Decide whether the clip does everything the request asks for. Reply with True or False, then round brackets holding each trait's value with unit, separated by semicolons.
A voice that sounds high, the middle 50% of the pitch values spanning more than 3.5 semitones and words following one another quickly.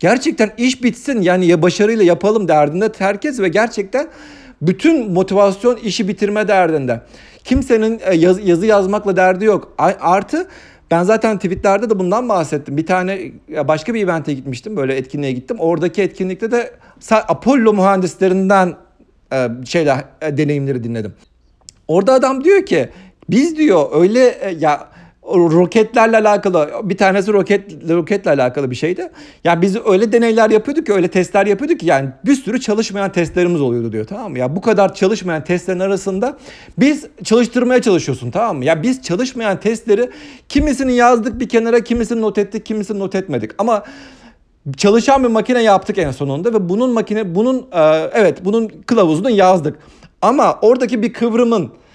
True (200 Hz; 5.2 semitones; 150 wpm)